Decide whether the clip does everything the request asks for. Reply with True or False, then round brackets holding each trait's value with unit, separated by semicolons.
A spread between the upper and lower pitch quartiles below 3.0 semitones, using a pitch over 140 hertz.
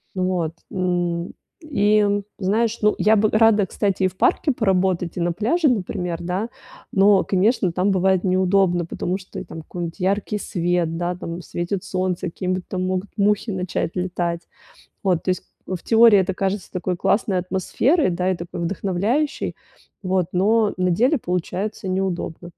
True (2.5 semitones; 185 Hz)